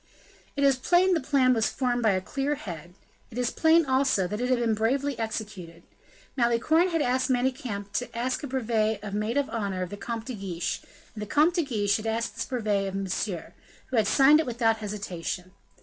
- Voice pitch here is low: No, high, 230 Hz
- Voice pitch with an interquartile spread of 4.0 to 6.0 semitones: Yes, average, 4.5 semitones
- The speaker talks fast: Yes, fast, 210 wpm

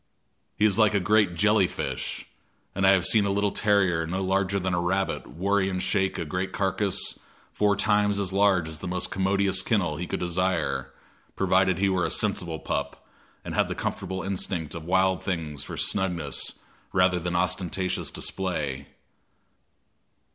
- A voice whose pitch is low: Yes, very low, 95 Hz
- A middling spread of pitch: No, narrow, 2.1 semitones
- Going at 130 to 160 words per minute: No, average, 170 wpm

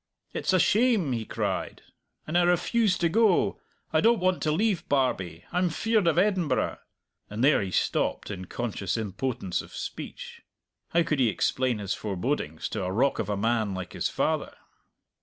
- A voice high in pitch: No, medium, 140 Hz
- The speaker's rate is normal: Yes, average, 175 wpm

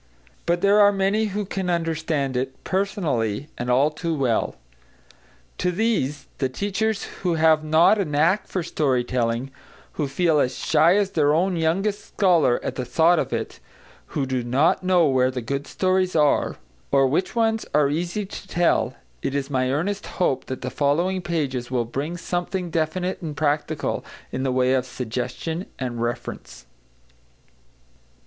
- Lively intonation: Yes, wide, 5.7 semitones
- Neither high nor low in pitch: Yes, medium, 155 Hz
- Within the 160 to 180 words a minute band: Yes, average, 165 wpm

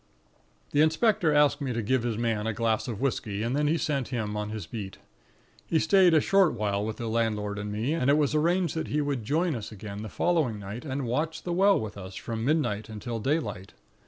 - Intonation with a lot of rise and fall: Yes, wide, 6.2 semitones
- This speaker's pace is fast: Yes, fast, 225 wpm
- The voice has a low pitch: Yes, low, 120 Hz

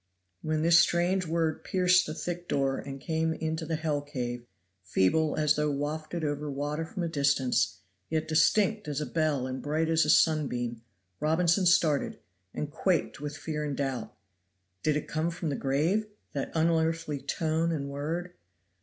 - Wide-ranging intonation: No, narrow, 2.5 semitones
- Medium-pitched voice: Yes, medium, 155 Hz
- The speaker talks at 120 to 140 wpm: No, average, 165 wpm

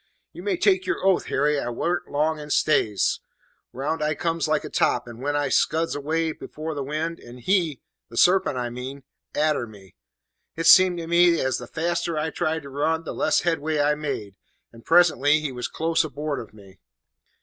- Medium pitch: Yes, medium, 155 Hz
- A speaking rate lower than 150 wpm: No, average, 195 wpm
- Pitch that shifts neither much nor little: Yes, average, 3.6 semitones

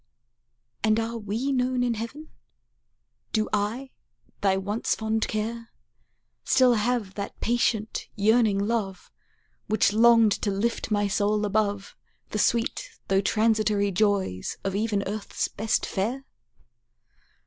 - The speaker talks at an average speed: No, slow, 120 wpm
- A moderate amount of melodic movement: No, narrow, 2.3 semitones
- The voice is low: No, high, 215 Hz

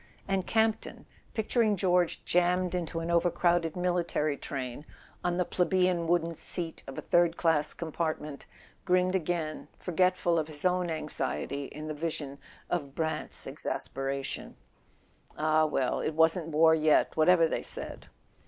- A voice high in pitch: No, medium, 165 Hz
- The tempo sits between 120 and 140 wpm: Yes, slow, 135 wpm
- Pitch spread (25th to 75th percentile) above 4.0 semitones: No, narrow, 2.6 semitones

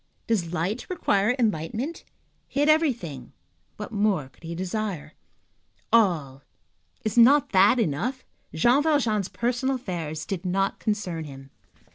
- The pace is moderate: No, slow, 120 wpm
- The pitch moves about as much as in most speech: No, wide, 6.6 semitones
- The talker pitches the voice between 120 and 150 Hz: No, high, 205 Hz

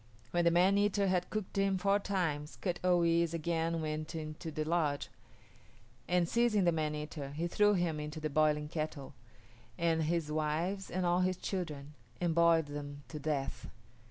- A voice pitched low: No, medium, 165 Hz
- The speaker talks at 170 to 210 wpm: Yes, average, 175 wpm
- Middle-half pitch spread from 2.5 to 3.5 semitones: Yes, average, 2.8 semitones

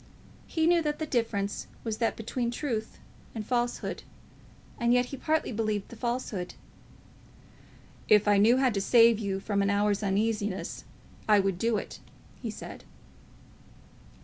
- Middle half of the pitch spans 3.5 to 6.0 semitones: No, average, 3.1 semitones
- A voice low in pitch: No, high, 225 Hz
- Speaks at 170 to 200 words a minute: No, average, 150 wpm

